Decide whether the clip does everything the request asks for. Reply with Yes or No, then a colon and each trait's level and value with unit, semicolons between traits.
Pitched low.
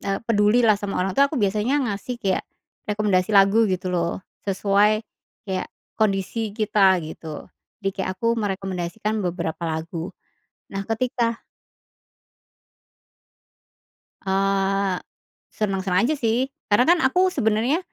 No: high, 200 Hz